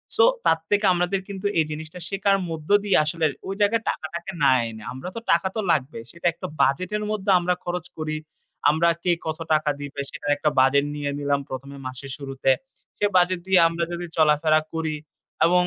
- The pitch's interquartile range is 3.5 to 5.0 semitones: Yes, average, 3.9 semitones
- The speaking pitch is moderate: Yes, medium, 160 Hz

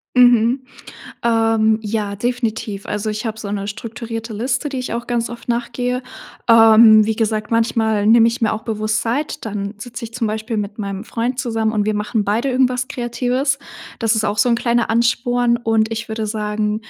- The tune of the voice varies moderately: No, narrow, 1.9 semitones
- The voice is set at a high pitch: Yes, high, 225 Hz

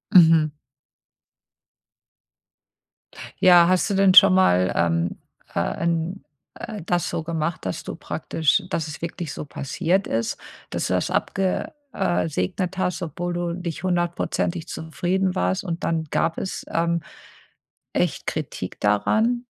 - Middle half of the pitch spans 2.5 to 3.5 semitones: Yes, average, 2.8 semitones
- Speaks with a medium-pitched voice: Yes, medium, 170 Hz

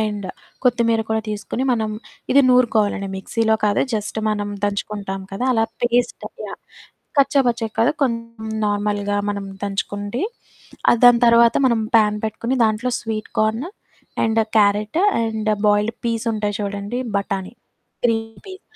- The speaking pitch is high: Yes, high, 220 Hz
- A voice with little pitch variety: Yes, narrow, 2.2 semitones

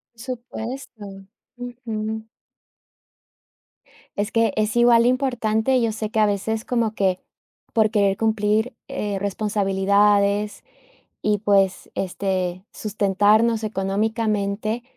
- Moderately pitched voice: No, high, 215 Hz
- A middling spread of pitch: No, narrow, 2.1 semitones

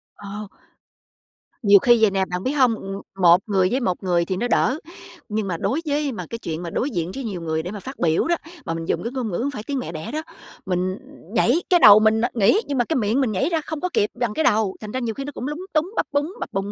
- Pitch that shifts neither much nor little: No, wide, 6.3 semitones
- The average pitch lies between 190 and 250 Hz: Yes, high, 220 Hz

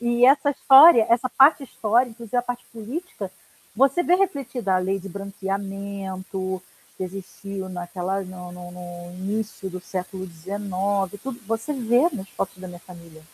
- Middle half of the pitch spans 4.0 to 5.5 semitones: Yes, average, 4.5 semitones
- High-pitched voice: Yes, high, 195 Hz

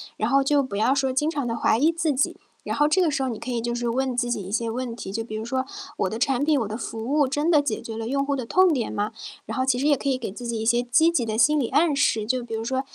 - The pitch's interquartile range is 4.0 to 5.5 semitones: No, average, 3.6 semitones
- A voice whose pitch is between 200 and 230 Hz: No, very high, 255 Hz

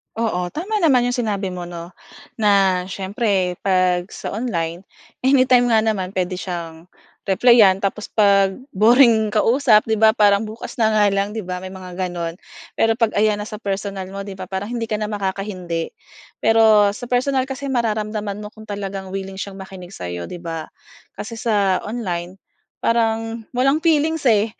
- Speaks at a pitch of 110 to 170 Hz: No, high, 205 Hz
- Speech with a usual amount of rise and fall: Yes, average, 3.1 semitones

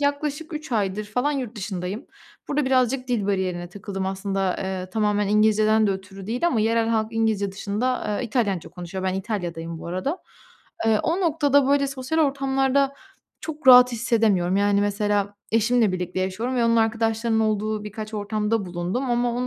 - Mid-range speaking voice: No, high, 215 Hz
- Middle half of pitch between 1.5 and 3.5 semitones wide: No, average, 4.4 semitones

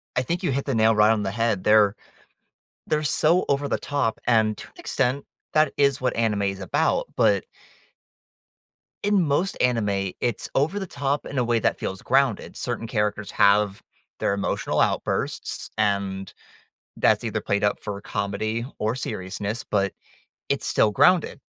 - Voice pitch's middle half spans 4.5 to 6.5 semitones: Yes, wide, 5.4 semitones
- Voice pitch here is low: Yes, low, 110 Hz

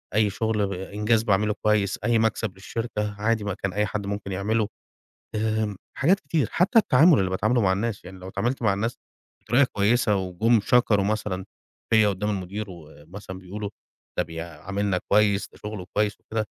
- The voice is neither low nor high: No, low, 105 Hz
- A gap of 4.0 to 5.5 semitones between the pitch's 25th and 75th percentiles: No, narrow, 2.4 semitones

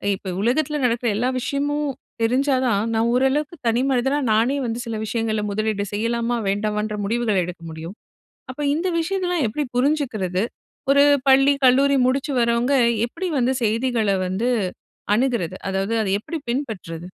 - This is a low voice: No, high, 240 Hz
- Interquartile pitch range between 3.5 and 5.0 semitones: Yes, average, 4.4 semitones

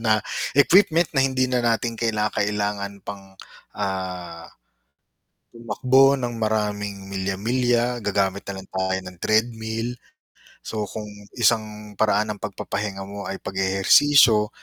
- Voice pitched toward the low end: Yes, low, 105 Hz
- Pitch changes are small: No, average, 3.1 semitones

